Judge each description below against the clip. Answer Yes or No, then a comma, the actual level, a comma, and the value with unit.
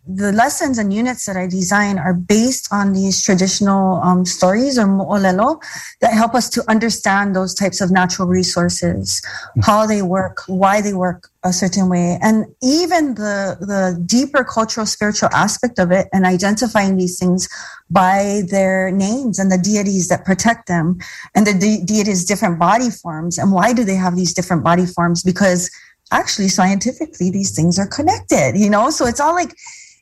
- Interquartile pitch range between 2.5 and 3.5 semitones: Yes, average, 3.0 semitones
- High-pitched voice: Yes, high, 195 Hz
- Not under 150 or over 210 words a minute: Yes, average, 175 wpm